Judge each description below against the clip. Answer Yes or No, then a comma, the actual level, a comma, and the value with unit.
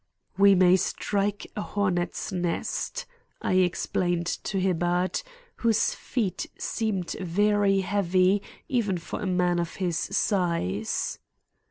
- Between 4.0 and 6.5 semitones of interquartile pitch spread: No, narrow, 2.5 semitones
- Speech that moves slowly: Yes, slow, 115 wpm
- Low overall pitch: No, medium, 185 Hz